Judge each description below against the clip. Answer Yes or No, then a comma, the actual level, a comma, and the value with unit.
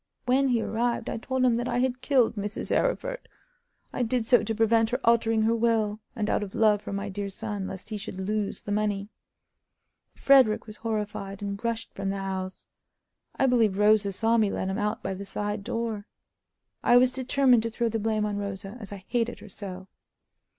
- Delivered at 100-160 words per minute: No, average, 200 wpm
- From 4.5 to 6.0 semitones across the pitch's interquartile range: No, narrow, 2.6 semitones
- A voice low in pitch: No, high, 220 Hz